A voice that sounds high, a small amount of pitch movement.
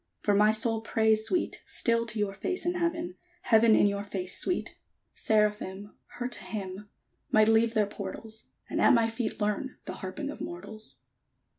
Yes: high, 220 Hz; narrow, 2.1 semitones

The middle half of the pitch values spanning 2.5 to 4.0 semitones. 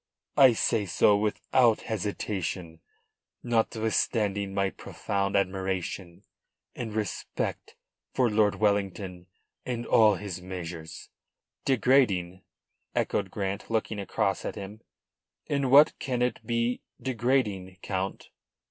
Yes: average, 3.5 semitones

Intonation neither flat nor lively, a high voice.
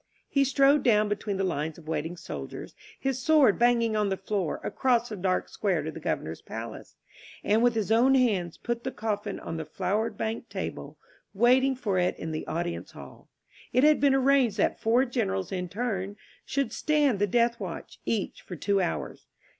Yes: average, 4.9 semitones; high, 220 Hz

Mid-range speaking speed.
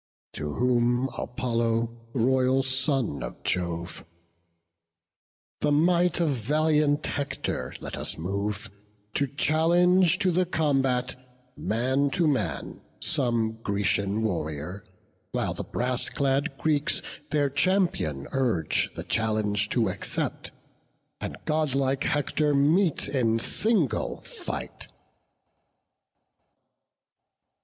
No: slow, 100 wpm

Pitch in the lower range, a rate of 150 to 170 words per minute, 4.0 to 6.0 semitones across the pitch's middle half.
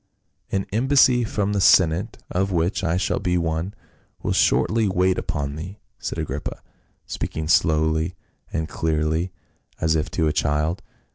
No: very low, 85 Hz; average, 160 wpm; average, 3.5 semitones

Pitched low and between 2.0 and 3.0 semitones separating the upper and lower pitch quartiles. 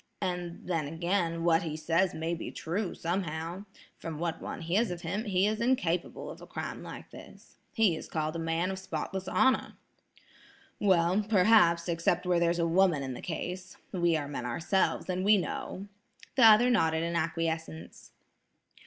No: medium, 170 Hz; narrow, 2.6 semitones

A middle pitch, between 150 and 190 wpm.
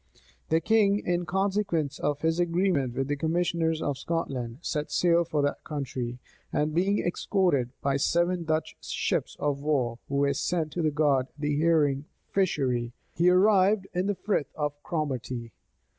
Yes: medium, 155 Hz; average, 155 wpm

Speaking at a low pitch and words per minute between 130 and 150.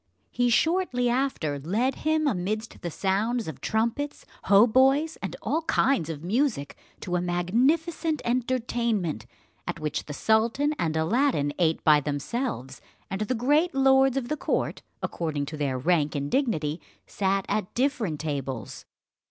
No: high, 220 Hz; average, 145 wpm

